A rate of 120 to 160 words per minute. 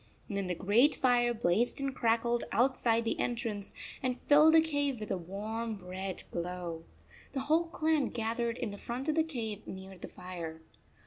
No: average, 175 wpm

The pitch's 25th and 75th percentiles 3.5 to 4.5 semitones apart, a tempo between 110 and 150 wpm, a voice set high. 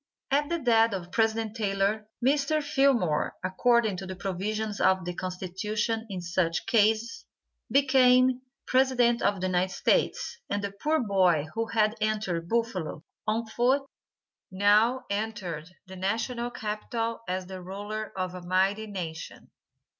Yes: average, 3.9 semitones; average, 140 wpm; high, 215 Hz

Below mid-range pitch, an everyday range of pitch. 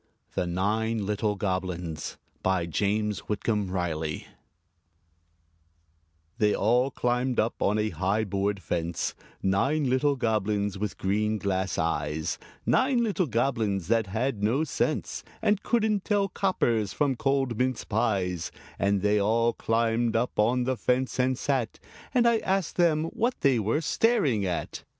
Yes: low, 110 Hz; average, 5.0 semitones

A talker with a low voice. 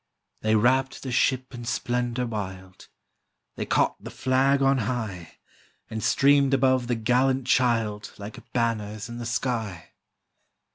Yes: low, 120 Hz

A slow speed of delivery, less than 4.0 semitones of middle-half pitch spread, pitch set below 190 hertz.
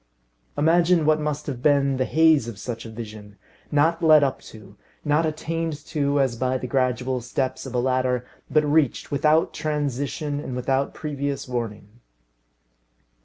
No: average, 155 wpm; average, 3.4 semitones; medium, 140 Hz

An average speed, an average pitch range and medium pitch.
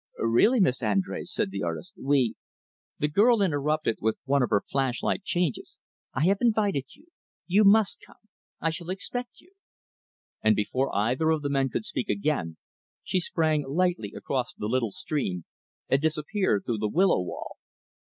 No: average, 170 wpm; wide, 8.1 semitones; medium, 145 Hz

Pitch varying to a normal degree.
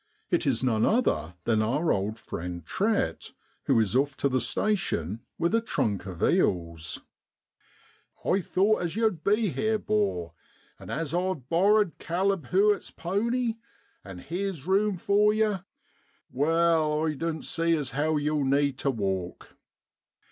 No: wide, 8.6 semitones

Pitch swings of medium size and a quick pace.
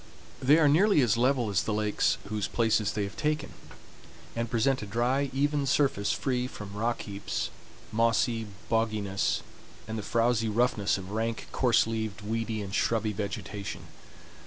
No: average, 3.1 semitones; average, 155 wpm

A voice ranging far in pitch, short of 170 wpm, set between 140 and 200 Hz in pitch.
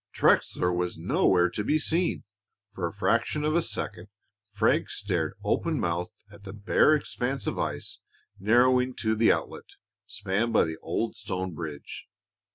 No: wide, 6.0 semitones; average, 155 wpm; low, 105 Hz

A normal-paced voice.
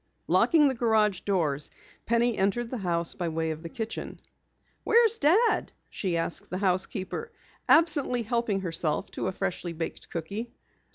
Yes: average, 150 wpm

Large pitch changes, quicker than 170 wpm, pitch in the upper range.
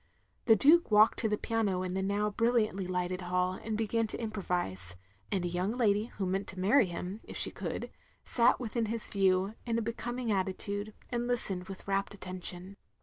No: average, 3.5 semitones; average, 190 wpm; high, 200 Hz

